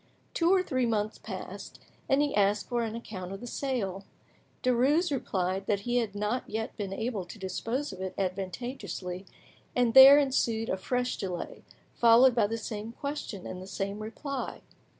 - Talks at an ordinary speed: Yes, average, 170 wpm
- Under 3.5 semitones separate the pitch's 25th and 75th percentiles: No, average, 4.5 semitones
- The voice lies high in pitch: Yes, high, 225 Hz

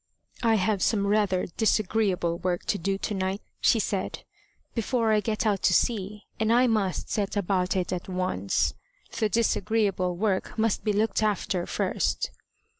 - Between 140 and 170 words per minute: Yes, average, 160 wpm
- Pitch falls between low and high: No, high, 200 Hz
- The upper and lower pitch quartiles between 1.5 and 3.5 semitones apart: Yes, average, 2.9 semitones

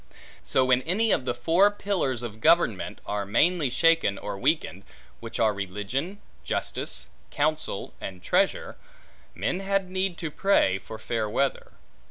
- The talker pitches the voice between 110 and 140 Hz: Yes, low, 135 Hz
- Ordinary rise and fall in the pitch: No, wide, 8.5 semitones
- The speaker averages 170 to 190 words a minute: No, average, 145 wpm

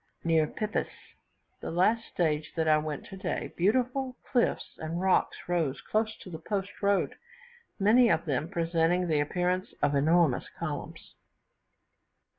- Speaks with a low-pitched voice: No, medium, 175 Hz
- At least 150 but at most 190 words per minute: No, slow, 135 wpm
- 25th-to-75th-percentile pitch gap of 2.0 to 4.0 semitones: No, average, 4.4 semitones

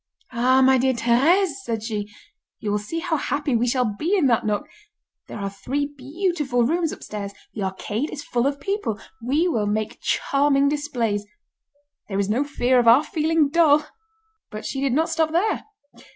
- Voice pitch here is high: Yes, very high, 265 Hz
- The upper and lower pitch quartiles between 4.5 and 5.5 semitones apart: Yes, average, 5.2 semitones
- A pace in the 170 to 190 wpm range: Yes, average, 180 wpm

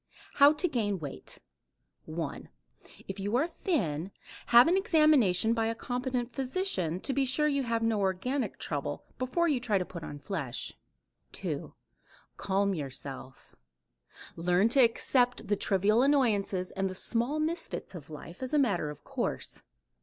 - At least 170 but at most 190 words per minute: No, average, 155 wpm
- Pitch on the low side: No, high, 225 Hz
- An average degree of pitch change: No, wide, 6.5 semitones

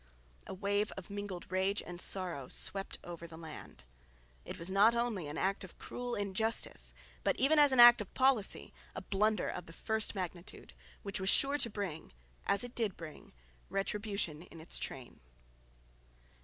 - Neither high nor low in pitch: No, high, 195 Hz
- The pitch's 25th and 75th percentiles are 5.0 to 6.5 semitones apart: No, average, 4.1 semitones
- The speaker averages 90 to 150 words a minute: No, average, 170 wpm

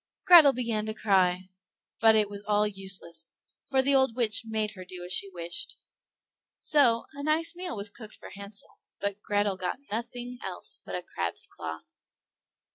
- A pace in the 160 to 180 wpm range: Yes, average, 170 wpm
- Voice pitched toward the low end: No, high, 210 Hz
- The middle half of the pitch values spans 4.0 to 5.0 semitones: Yes, average, 4.6 semitones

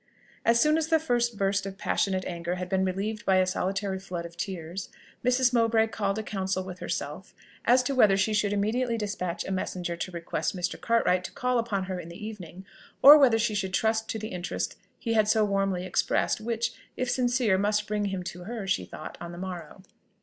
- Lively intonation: No, average, 3.4 semitones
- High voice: Yes, high, 200 Hz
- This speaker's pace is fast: Yes, fast, 210 wpm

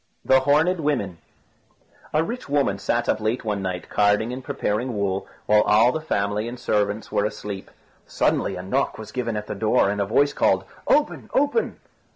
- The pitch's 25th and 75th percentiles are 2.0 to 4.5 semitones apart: No, average, 5.1 semitones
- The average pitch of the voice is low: Yes, low, 110 Hz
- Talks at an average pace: Yes, average, 185 wpm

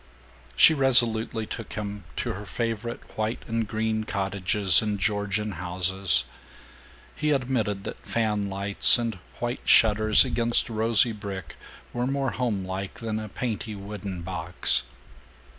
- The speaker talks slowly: Yes, slow, 125 wpm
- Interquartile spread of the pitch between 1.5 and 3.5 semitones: Yes, average, 2.8 semitones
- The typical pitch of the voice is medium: No, low, 105 Hz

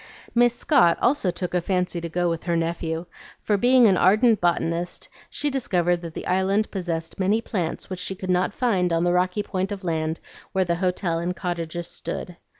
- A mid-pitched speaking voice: Yes, medium, 180 Hz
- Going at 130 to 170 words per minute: No, average, 195 wpm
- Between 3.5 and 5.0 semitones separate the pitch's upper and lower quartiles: No, average, 2.7 semitones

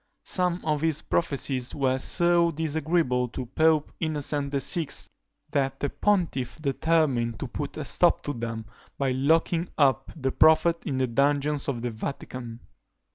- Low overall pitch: No, medium, 145 Hz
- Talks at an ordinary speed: Yes, average, 145 wpm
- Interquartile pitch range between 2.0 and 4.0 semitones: Yes, average, 3.6 semitones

